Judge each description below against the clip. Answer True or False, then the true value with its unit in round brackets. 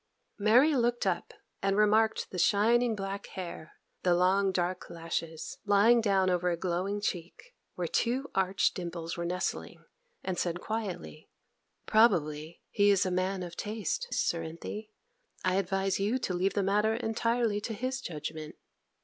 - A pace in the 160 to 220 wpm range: False (150 wpm)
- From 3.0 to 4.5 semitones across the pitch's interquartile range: True (3.6 semitones)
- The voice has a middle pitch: False (195 Hz)